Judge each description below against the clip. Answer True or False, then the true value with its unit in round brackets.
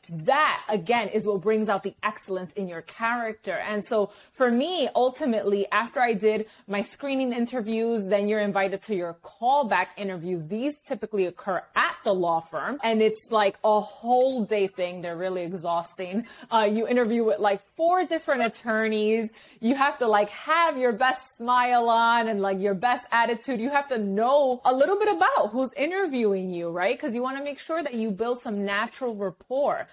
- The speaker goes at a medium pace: True (185 wpm)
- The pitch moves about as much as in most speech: True (4.1 semitones)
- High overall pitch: True (220 Hz)